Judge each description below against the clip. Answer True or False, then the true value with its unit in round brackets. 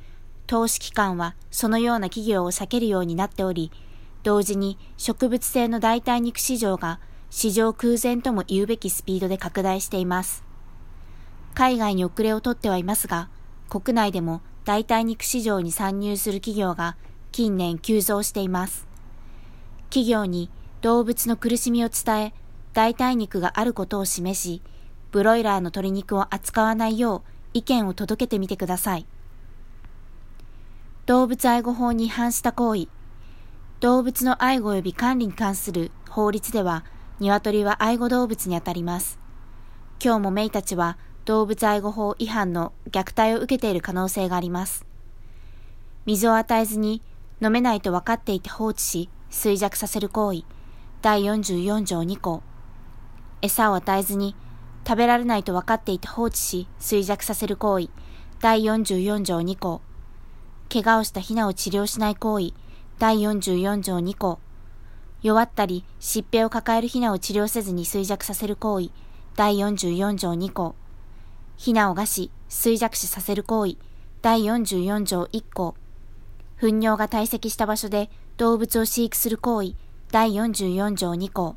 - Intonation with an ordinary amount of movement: True (3.8 semitones)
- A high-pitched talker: True (205 Hz)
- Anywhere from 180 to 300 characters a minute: True (270 characters per minute)